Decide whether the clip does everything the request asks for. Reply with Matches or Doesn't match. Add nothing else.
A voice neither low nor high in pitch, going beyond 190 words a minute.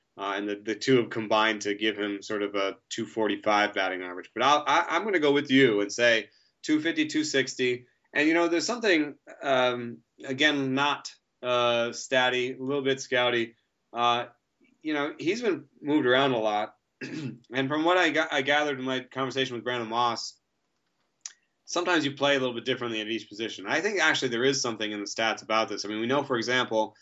Doesn't match